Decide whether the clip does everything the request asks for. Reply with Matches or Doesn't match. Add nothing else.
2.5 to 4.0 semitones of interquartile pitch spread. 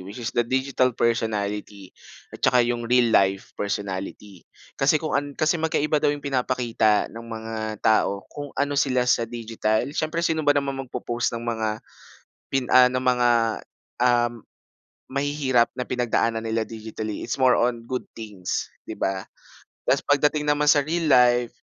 Matches